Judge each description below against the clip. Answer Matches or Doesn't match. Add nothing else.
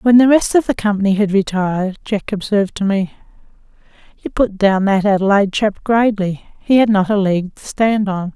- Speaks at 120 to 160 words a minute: Doesn't match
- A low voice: Doesn't match